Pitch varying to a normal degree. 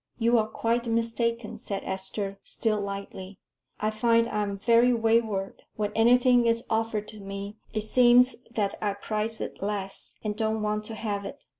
No: narrow, 2.3 semitones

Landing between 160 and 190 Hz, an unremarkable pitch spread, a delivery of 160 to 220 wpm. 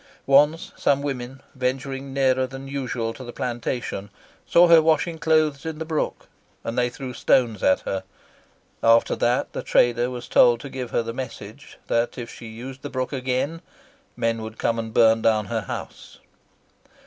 No: low, 125 Hz; average, 3.0 semitones; average, 170 wpm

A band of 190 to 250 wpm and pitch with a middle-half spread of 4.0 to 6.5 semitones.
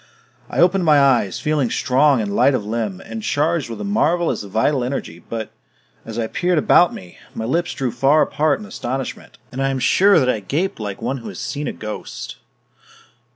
Yes: average, 200 wpm; wide, 5.5 semitones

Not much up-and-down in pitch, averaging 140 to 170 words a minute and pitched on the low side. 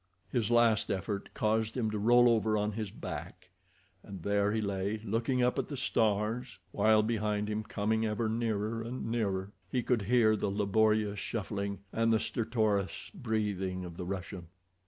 Yes: narrow, 2.2 semitones; average, 165 wpm; low, 110 Hz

